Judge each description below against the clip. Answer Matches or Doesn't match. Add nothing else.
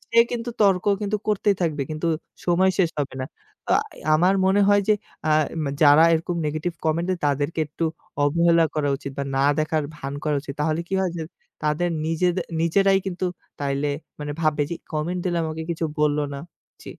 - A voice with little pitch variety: Doesn't match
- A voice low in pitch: Doesn't match